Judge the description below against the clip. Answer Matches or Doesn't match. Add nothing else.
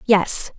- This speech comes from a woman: Matches